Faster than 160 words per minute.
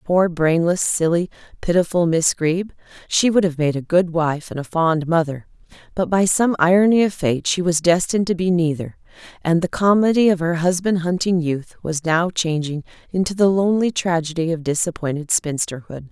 Yes: average, 175 wpm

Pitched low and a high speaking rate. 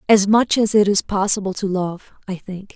No: high, 200 Hz; fast, 220 wpm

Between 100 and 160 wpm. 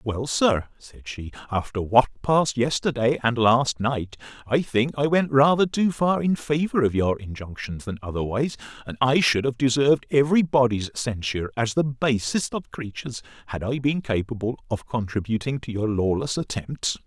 No: average, 170 wpm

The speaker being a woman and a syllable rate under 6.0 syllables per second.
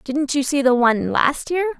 Yes: female; 4.9 syllables/s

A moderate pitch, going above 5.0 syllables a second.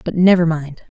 No: medium, 165 Hz; 4.9 syllables/s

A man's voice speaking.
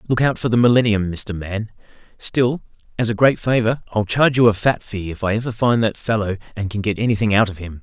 Yes: male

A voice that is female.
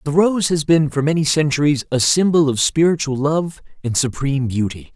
No: male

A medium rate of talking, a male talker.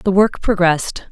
No: average, 160 wpm; female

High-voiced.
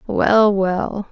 Yes: high, 200 Hz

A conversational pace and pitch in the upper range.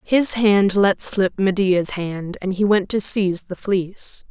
Yes: average, 180 wpm; high, 195 Hz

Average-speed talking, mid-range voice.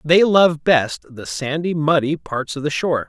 Yes: average, 195 wpm; medium, 150 Hz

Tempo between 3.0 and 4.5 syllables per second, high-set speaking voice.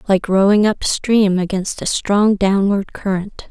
Yes: 3.9 syllables/s; high, 200 Hz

